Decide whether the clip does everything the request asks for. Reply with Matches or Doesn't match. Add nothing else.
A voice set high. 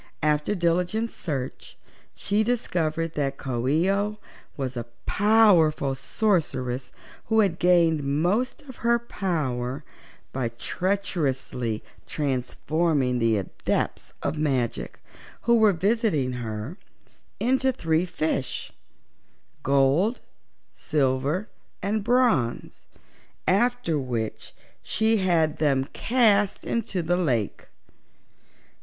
Doesn't match